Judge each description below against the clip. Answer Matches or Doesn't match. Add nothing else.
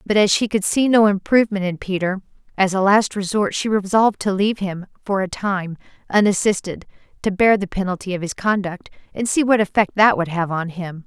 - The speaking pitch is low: Doesn't match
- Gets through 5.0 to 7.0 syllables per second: Matches